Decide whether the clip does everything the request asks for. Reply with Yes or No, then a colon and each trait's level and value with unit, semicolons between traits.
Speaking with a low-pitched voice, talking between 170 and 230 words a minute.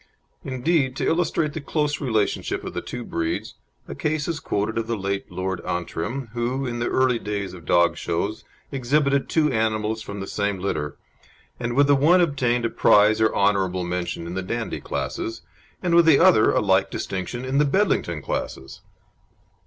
Yes: low, 115 Hz; average, 180 wpm